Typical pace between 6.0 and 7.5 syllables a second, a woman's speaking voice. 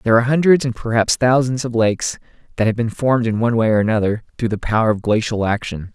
No: 6.8 syllables/s; male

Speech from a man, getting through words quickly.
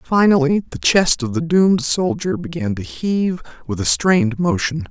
No: male; average, 170 wpm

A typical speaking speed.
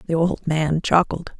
Yes: average, 170 wpm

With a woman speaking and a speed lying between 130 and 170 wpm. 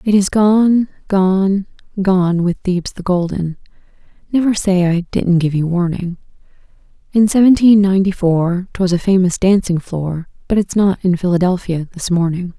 Yes: female; average, 155 wpm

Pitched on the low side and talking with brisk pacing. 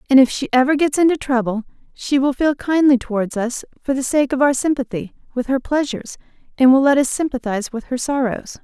No: very high, 260 Hz; fast, 210 wpm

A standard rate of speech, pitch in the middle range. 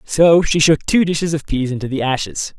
No: fast, 230 wpm; medium, 155 Hz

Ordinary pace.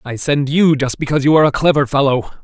No: fast, 245 wpm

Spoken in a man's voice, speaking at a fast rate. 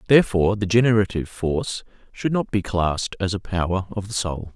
No: male; average, 185 wpm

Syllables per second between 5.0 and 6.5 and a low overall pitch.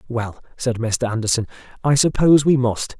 Yes: 5.2 syllables/s; low, 125 Hz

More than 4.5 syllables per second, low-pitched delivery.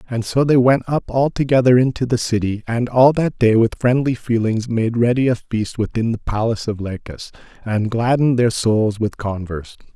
Yes: 5.2 syllables/s; low, 115 Hz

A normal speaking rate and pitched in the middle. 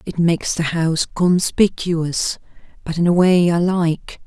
Yes: average, 155 wpm; medium, 170 Hz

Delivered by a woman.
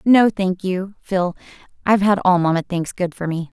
Yes: female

